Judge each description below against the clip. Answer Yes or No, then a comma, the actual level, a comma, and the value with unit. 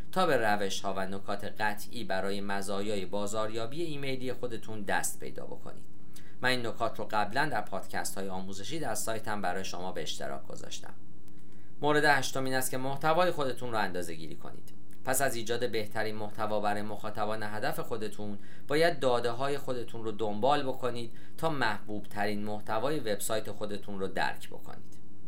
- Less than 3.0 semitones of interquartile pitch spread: No, average, 3.4 semitones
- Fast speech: Yes, fast, 160 wpm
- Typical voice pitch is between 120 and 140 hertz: No, low, 105 Hz